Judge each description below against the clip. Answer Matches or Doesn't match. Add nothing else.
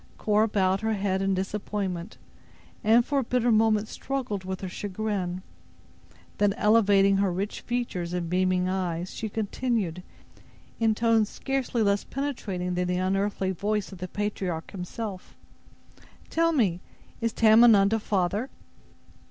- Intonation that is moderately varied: Matches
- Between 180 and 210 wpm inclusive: Doesn't match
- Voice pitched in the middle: Doesn't match